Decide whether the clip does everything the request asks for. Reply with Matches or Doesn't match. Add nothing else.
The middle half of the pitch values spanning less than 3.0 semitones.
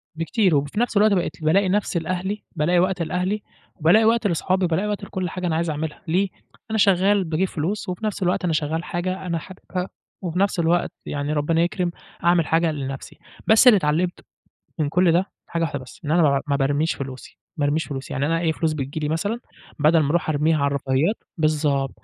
Doesn't match